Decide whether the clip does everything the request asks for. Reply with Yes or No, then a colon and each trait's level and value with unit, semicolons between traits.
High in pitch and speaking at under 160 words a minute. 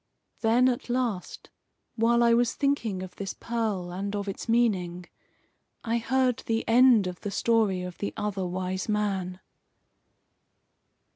Yes: high, 210 Hz; average, 140 wpm